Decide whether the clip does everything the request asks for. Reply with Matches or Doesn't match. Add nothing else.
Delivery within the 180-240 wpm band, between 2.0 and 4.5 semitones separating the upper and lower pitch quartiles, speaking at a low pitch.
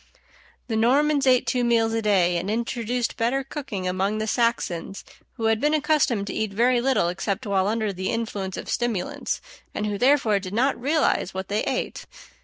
Doesn't match